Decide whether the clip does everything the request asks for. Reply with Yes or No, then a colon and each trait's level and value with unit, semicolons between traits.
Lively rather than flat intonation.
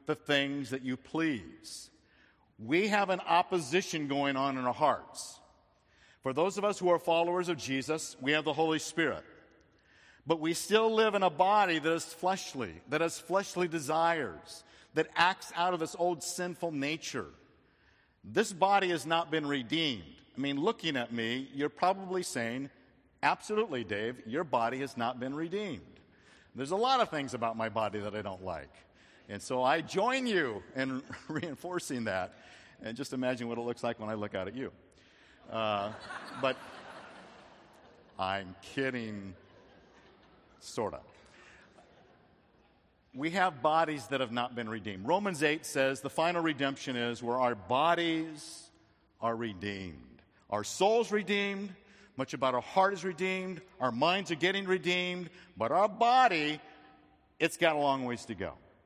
Yes: wide, 6.2 semitones